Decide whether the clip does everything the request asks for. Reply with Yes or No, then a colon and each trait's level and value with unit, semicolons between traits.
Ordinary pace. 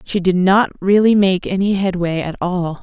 Yes: average, 190 wpm